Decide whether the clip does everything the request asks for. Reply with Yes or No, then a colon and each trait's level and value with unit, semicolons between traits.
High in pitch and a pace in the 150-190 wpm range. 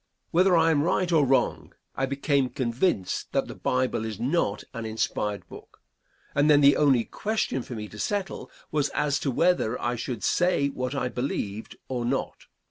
No: low, 135 Hz; average, 180 wpm